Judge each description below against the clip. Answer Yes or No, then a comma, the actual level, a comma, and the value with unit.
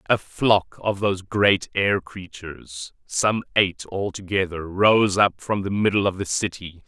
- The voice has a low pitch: Yes, very low, 95 Hz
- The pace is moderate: Yes, average, 155 wpm